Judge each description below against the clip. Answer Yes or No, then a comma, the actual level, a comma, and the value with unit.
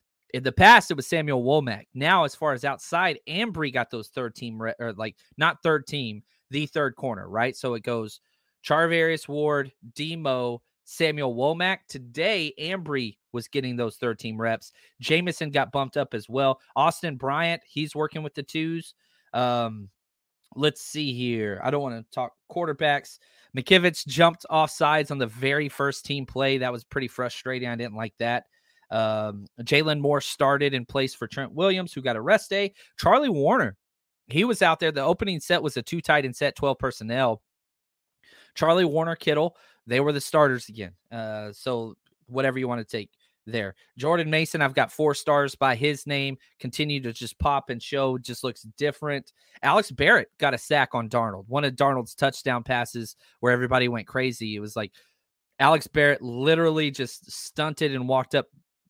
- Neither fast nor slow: Yes, average, 180 wpm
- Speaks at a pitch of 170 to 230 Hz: No, low, 135 Hz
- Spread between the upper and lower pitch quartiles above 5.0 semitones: No, average, 4.1 semitones